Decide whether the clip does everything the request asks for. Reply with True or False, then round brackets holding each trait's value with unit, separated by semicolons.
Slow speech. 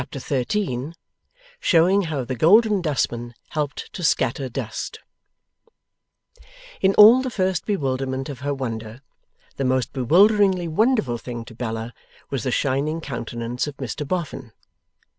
True (130 wpm)